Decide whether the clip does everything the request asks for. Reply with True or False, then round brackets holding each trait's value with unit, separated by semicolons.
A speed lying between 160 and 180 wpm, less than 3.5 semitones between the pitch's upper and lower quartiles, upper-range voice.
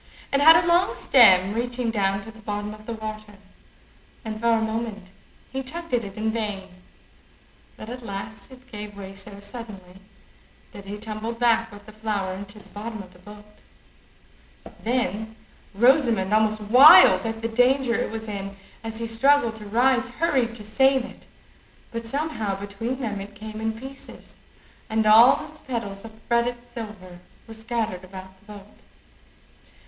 True (165 wpm; 2.7 semitones; 220 Hz)